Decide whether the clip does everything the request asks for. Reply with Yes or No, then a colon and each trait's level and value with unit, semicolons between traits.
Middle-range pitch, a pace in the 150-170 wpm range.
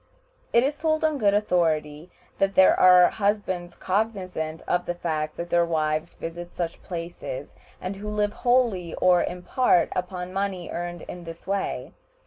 Yes: medium, 180 Hz; average, 160 wpm